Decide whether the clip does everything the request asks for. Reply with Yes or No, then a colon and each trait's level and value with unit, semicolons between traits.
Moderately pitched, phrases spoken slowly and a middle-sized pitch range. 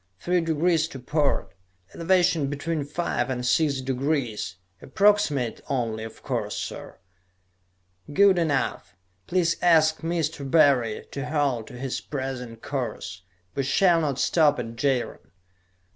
Yes: medium, 145 Hz; slow, 125 wpm; average, 4.6 semitones